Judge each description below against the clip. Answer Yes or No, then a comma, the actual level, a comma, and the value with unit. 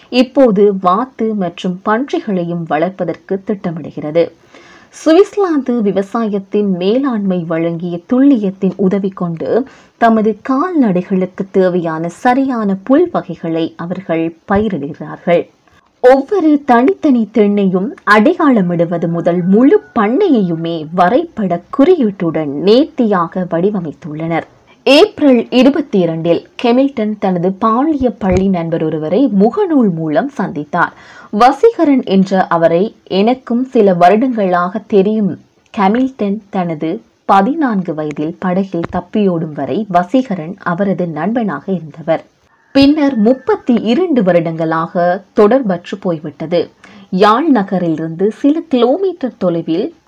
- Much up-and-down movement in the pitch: Yes, wide, 6.1 semitones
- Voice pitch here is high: Yes, high, 200 Hz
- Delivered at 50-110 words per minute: Yes, average, 85 wpm